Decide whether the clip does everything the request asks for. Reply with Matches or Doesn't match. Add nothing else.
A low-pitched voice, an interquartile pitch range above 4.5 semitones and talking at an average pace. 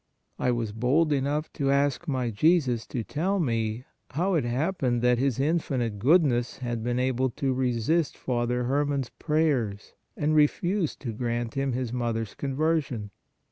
Doesn't match